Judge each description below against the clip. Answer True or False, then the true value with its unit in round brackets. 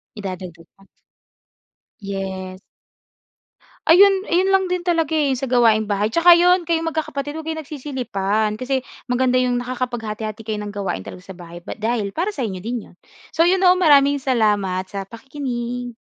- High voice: True (245 Hz)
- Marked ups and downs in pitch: True (7.4 semitones)